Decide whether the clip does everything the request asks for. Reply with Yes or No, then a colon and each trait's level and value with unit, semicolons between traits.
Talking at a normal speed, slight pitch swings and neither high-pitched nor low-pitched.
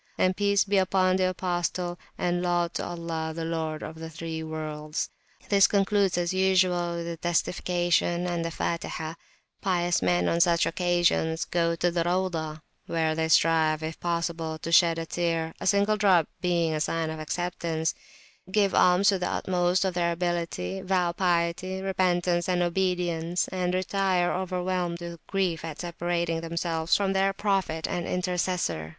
Yes: average, 160 wpm; narrow, 1.9 semitones; medium, 175 Hz